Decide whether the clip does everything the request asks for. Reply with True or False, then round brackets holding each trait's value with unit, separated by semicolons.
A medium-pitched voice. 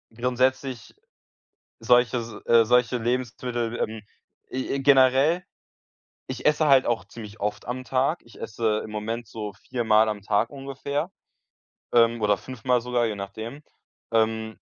False (120 Hz)